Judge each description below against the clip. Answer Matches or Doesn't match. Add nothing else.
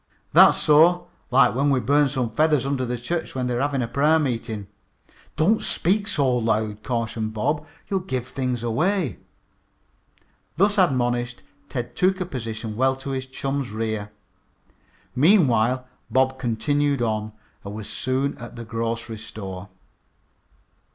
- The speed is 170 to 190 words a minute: Doesn't match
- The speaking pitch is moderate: Doesn't match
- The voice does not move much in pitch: Doesn't match